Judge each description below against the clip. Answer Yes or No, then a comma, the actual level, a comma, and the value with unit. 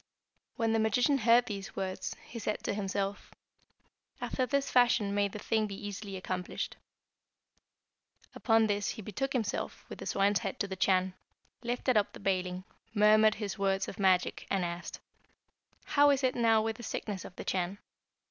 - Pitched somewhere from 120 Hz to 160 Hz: No, high, 205 Hz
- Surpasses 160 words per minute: Yes, average, 170 wpm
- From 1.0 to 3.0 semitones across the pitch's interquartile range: Yes, average, 2.7 semitones